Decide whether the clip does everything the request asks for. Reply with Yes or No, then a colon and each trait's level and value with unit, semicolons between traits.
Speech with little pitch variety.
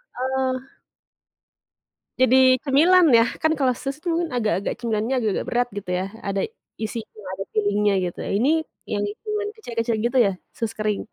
No: average, 3.8 semitones